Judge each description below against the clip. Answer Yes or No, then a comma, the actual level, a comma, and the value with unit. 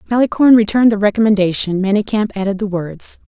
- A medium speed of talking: Yes, average, 145 wpm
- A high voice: Yes, high, 205 Hz